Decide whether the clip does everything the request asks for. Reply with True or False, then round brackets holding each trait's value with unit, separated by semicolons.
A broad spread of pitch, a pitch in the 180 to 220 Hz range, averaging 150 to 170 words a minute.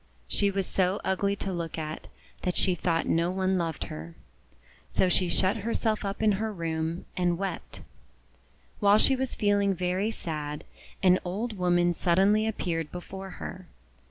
False (2.7 semitones; 185 Hz; 160 wpm)